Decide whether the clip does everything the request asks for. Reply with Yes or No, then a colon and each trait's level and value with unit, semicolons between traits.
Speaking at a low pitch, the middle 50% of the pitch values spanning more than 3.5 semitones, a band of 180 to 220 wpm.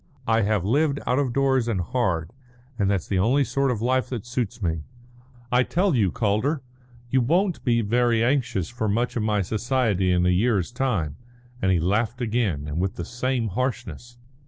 Yes: low, 115 Hz; average, 4.6 semitones; average, 185 wpm